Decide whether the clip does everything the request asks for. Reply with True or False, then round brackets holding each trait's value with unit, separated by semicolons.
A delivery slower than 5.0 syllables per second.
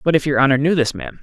False (7.1 syllables/s)